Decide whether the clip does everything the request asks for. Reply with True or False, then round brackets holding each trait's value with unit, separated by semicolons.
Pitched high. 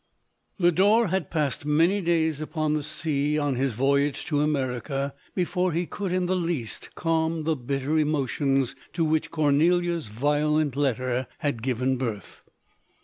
False (150 Hz)